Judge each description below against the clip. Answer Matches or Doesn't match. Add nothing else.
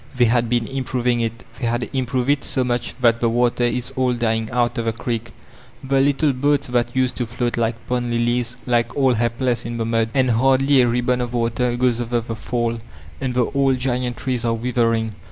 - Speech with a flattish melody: Matches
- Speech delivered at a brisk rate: Matches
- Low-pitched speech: Matches